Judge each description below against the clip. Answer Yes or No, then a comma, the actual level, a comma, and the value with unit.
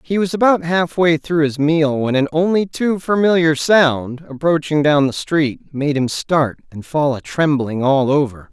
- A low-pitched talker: No, medium, 150 Hz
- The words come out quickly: No, average, 185 wpm